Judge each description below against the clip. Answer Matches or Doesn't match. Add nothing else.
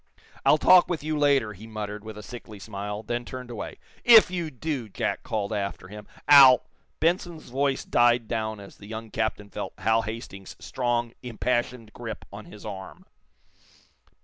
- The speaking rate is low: Doesn't match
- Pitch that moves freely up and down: Doesn't match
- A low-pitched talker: Matches